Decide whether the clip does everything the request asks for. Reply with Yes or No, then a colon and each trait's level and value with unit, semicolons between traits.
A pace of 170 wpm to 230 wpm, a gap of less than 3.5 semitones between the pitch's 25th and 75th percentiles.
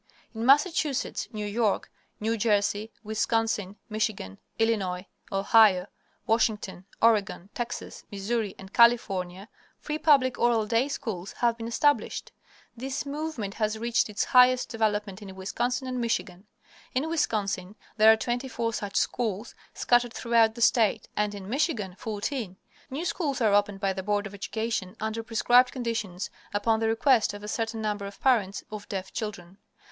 No: average, 150 wpm; average, 3.0 semitones